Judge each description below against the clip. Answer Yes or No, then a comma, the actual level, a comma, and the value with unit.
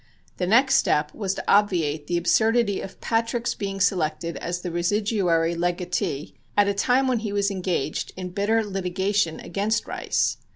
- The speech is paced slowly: No, average, 165 wpm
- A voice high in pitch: Yes, high, 195 Hz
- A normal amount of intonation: Yes, average, 3.4 semitones